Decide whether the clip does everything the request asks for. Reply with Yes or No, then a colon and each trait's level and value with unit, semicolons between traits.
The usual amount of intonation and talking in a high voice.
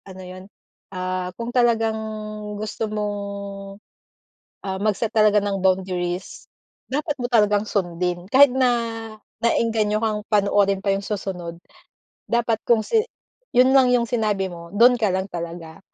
Yes: average, 3.6 semitones; high, 210 Hz